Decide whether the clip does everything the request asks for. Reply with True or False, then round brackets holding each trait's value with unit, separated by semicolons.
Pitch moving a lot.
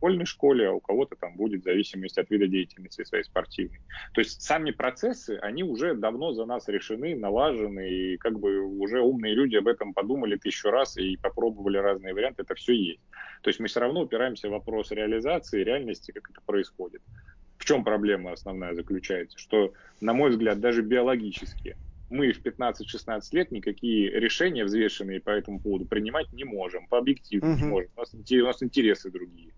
False (4.3 semitones)